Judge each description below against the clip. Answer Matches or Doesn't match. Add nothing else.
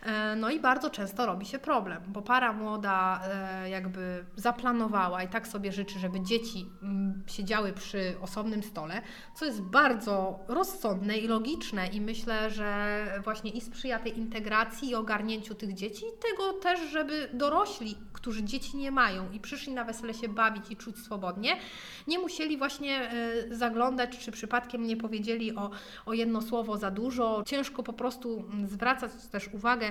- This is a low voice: Doesn't match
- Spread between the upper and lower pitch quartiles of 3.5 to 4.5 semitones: Doesn't match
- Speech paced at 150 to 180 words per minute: Matches